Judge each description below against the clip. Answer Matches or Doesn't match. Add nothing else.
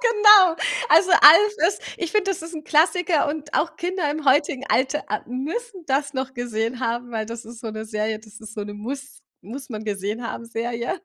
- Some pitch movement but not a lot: Doesn't match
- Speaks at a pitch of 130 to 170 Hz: Doesn't match